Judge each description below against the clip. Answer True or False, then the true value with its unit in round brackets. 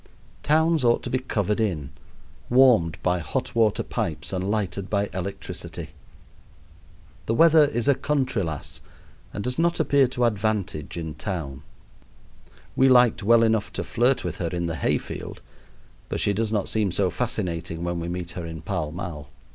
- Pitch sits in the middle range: False (100 Hz)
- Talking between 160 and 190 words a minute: True (170 wpm)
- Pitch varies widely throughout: True (5.9 semitones)